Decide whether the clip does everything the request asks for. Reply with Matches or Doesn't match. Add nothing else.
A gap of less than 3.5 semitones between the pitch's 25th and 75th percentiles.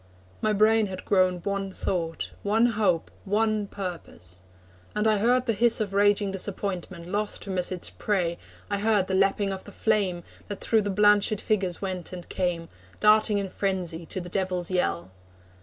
Matches